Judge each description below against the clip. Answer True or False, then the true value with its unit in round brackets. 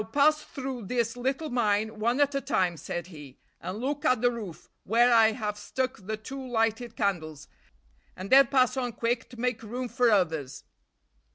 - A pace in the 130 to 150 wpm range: False (185 wpm)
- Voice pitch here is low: False (230 Hz)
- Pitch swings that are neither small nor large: True (3.6 semitones)